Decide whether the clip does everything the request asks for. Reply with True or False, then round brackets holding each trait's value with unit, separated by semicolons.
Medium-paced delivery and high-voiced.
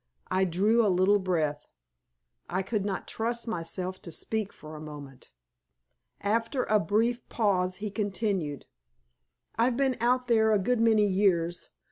True (145 wpm; 205 Hz)